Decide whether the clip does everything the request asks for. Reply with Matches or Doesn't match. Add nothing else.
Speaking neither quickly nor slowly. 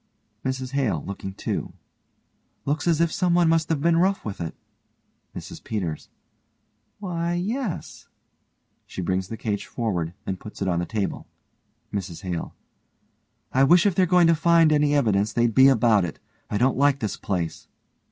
Matches